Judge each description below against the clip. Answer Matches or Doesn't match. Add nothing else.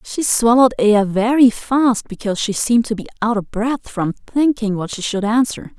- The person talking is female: Matches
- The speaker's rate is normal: Matches